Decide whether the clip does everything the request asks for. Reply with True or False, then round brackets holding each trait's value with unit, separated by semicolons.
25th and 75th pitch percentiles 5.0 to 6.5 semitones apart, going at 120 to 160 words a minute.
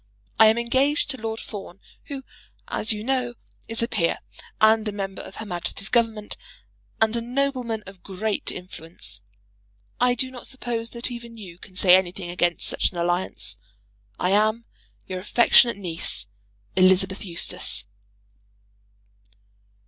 False (4.3 semitones; 140 wpm)